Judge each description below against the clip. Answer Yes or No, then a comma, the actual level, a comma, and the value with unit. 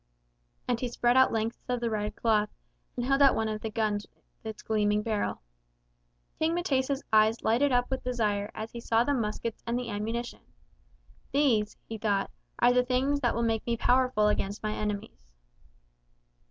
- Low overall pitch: No, high, 230 Hz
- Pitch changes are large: No, average, 2.8 semitones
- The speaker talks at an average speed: Yes, average, 180 wpm